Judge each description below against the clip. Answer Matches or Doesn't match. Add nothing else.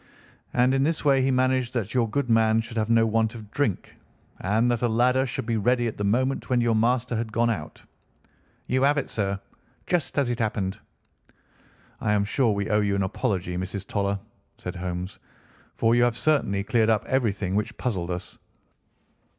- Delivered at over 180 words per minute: Matches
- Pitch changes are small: Doesn't match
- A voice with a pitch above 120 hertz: Doesn't match